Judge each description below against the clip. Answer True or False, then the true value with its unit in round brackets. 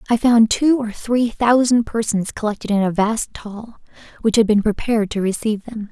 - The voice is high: True (220 Hz)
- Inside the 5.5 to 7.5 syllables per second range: False (5.1 syllables/s)